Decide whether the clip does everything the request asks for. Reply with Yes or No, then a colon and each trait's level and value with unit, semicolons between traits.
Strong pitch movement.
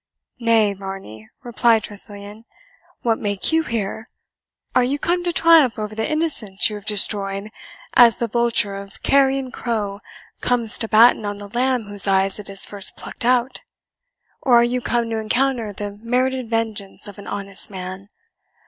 No: average, 3.4 semitones